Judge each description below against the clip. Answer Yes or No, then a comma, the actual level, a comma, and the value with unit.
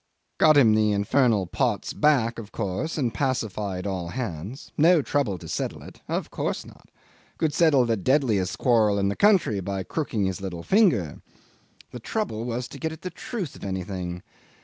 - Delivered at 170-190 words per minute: Yes, average, 175 wpm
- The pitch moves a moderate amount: No, wide, 6.7 semitones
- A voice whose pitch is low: Yes, low, 115 Hz